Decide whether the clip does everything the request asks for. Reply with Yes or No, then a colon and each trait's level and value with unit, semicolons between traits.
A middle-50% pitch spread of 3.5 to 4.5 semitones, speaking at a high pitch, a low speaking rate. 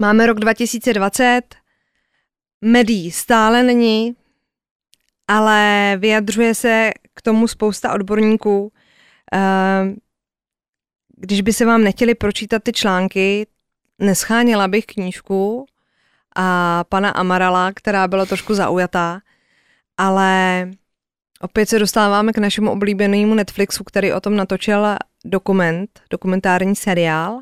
No: average, 2.7 semitones; high, 205 Hz; slow, 100 wpm